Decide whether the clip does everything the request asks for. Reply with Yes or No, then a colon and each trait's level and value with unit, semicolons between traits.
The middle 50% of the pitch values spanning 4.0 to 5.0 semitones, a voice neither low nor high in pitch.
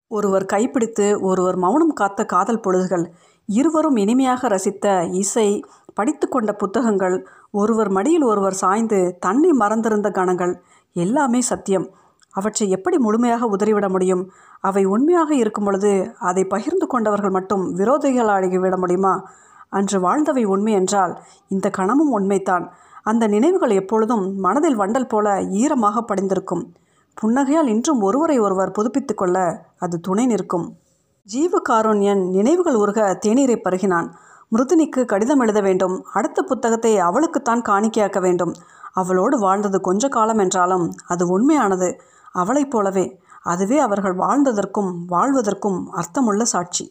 No: average, 4.6 semitones; high, 205 Hz